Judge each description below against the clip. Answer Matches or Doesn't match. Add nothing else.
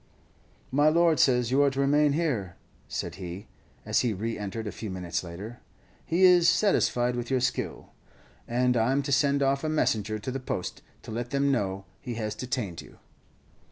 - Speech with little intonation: Doesn't match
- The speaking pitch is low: Matches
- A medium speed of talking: Matches